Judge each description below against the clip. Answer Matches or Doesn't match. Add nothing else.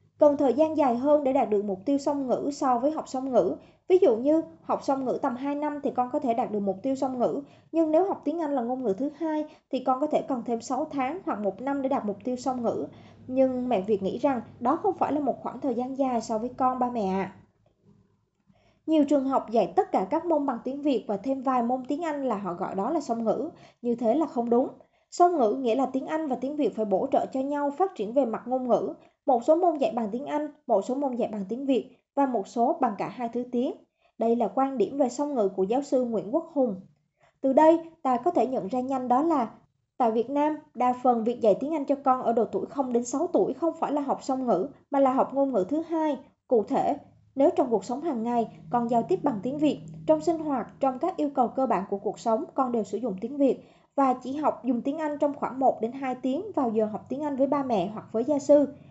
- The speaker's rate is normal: Doesn't match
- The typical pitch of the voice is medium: Doesn't match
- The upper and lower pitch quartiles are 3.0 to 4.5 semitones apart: Matches